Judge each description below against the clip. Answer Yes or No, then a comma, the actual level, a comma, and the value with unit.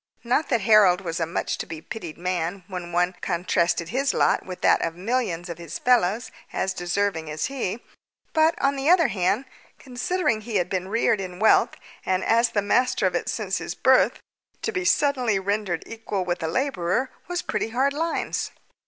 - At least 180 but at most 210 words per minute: Yes, average, 190 wpm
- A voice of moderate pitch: No, high, 205 Hz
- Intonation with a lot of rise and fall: Yes, wide, 6.1 semitones